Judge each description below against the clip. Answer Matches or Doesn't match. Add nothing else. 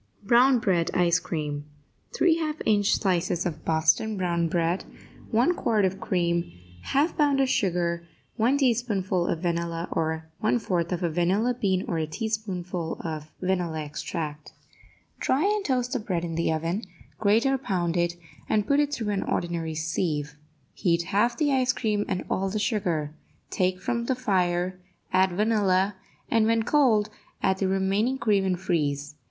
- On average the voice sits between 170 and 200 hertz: Matches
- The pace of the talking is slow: Doesn't match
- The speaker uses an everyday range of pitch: Matches